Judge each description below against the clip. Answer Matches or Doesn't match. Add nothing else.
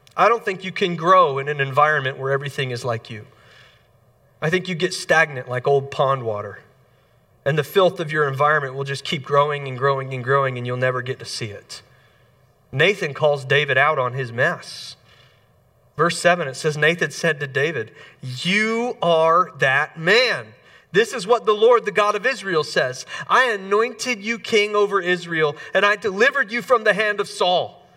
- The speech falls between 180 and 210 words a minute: Matches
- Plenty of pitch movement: Matches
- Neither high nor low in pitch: Matches